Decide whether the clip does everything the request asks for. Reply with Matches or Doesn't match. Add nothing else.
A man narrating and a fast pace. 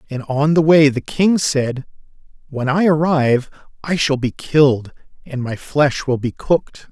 Doesn't match